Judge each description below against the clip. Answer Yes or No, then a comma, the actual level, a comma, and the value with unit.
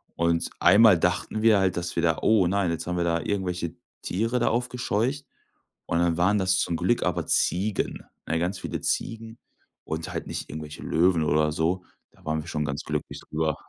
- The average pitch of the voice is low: Yes, very low, 90 Hz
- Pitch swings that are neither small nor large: Yes, average, 4.0 semitones